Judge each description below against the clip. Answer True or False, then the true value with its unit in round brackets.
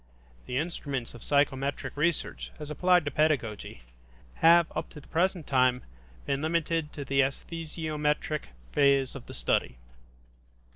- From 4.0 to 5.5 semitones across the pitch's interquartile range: False (3.1 semitones)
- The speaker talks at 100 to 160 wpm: True (135 wpm)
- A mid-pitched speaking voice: True (145 Hz)